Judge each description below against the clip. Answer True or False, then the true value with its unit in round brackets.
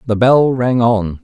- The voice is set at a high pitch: False (115 Hz)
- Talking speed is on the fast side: False (195 wpm)